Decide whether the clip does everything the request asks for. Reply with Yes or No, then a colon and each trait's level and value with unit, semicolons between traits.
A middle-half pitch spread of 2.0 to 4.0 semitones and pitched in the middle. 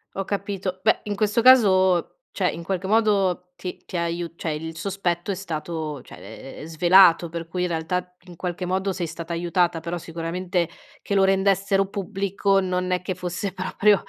Yes: narrow, 2.4 semitones; medium, 180 Hz